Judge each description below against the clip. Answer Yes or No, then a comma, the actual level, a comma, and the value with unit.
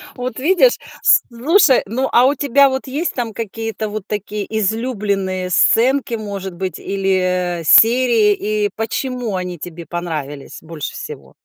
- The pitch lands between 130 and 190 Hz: No, high, 215 Hz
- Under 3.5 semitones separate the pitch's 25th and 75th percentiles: No, average, 5.1 semitones